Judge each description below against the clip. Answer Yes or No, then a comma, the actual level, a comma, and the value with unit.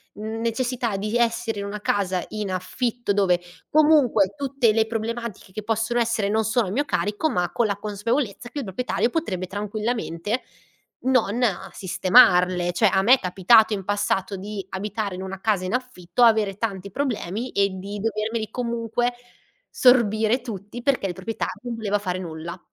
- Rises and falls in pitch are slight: No, average, 3.4 semitones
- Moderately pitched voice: No, high, 215 Hz